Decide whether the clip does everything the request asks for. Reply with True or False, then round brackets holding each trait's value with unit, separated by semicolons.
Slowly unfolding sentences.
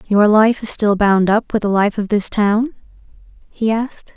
False (200 wpm)